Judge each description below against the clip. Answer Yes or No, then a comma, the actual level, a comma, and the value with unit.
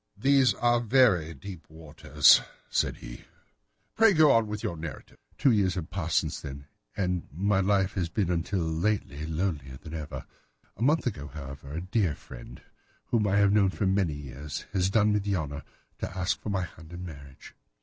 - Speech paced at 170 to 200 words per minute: Yes, average, 180 wpm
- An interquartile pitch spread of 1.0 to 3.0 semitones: No, average, 4.9 semitones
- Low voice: Yes, very low, 90 Hz